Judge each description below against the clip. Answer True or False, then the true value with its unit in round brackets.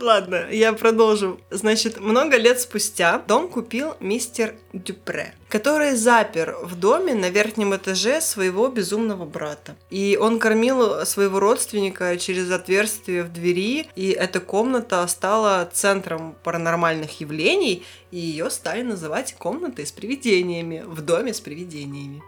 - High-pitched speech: True (200 Hz)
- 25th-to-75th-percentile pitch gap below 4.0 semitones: False (4.3 semitones)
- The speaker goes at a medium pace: True (130 wpm)